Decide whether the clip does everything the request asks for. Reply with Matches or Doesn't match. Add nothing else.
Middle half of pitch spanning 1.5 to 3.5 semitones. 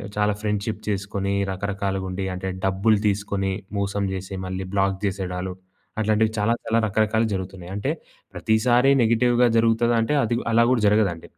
Matches